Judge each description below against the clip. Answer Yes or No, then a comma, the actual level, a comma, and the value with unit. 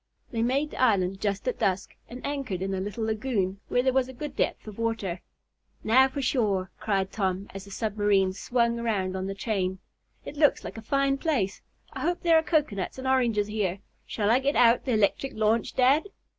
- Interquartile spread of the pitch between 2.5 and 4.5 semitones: No, average, 5.0 semitones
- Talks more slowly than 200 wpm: No, fast, 205 wpm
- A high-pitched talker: Yes, high, 225 Hz